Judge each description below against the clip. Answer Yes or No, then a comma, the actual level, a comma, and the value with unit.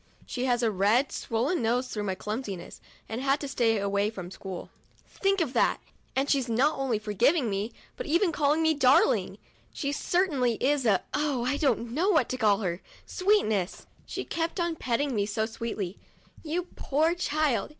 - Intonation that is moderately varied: No, wide, 5.7 semitones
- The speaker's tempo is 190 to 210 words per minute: Yes, average, 195 wpm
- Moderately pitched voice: No, very high, 255 Hz